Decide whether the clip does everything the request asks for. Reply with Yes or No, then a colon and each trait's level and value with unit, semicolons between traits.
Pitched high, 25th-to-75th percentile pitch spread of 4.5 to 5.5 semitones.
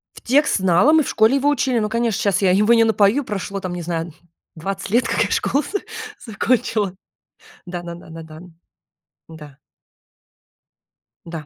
Yes: high, 200 Hz; average, 5.2 semitones